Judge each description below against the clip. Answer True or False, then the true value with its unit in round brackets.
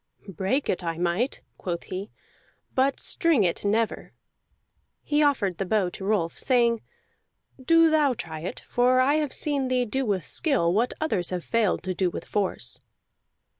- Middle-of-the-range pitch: False (220 Hz)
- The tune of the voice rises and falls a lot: True (6.5 semitones)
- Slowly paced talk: False (165 wpm)